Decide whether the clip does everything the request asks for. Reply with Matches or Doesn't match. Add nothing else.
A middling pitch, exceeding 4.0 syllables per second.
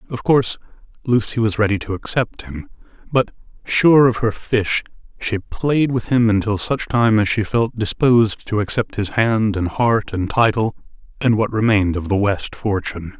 Doesn't match